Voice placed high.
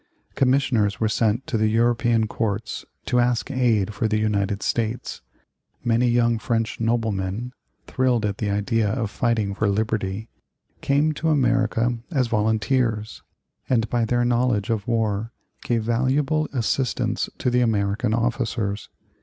No: low, 115 Hz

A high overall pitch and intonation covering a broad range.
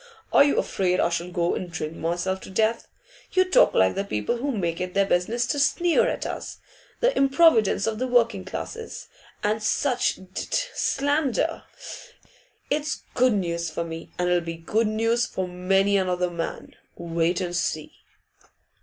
Yes: high, 195 Hz; wide, 5.8 semitones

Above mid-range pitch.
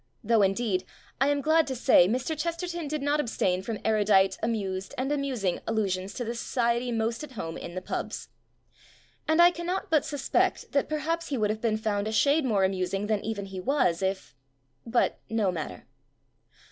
Yes: high, 225 Hz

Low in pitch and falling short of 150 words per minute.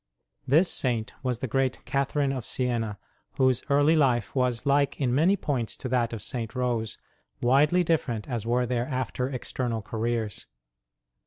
No: low, 125 Hz; average, 155 wpm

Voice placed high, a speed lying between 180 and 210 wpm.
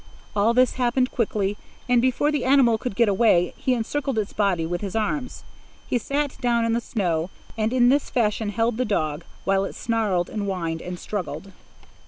Yes: high, 220 Hz; average, 190 wpm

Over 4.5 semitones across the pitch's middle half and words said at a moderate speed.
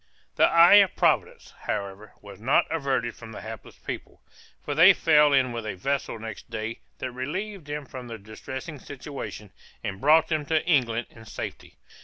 Yes: average, 5.3 semitones; average, 175 wpm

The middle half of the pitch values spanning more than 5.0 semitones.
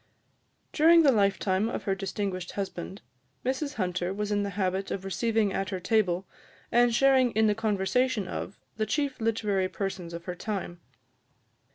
No: average, 3.2 semitones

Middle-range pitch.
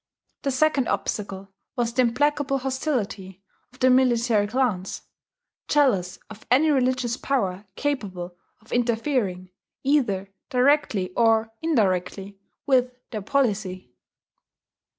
No: high, 235 Hz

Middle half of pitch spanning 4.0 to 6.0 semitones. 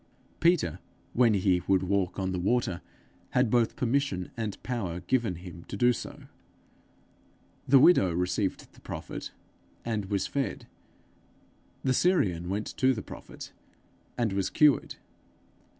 Yes: average, 5.3 semitones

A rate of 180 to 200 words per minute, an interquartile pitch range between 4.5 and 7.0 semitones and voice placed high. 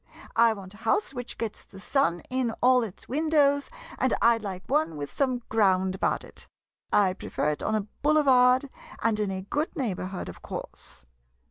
Yes: average, 190 wpm; wide, 5.4 semitones; high, 225 Hz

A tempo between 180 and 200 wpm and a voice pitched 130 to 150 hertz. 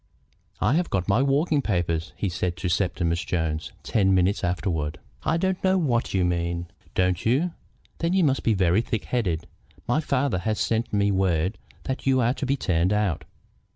No: average, 185 wpm; low, 100 Hz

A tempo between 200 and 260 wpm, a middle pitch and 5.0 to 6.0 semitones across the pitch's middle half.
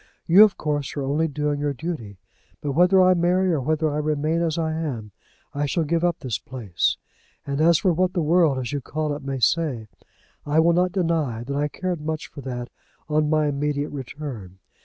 No: fast, 205 wpm; medium, 150 Hz; average, 3.3 semitones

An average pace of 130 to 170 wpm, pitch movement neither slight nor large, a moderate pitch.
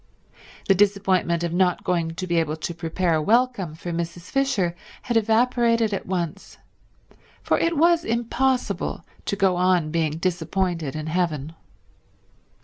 Yes: average, 140 wpm; average, 4.9 semitones; medium, 180 Hz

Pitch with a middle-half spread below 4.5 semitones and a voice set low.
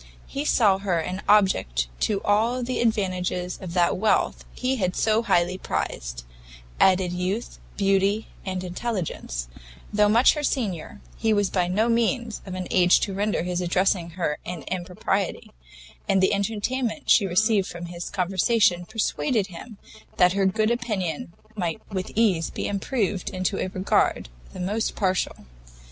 No: average, 3.3 semitones; high, 190 Hz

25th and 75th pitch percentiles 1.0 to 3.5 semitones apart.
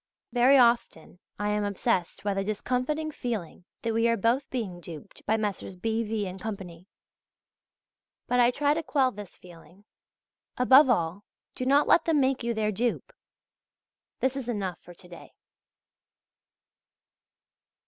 No: average, 4.5 semitones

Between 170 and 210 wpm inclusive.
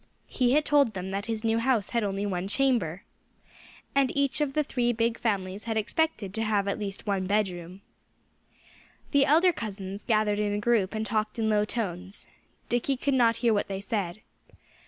Yes: average, 185 wpm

